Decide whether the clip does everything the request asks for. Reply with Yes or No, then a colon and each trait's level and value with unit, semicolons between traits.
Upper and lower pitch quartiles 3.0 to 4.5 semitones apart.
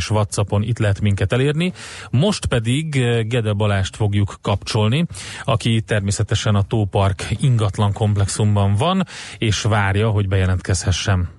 No: narrow, 2.6 semitones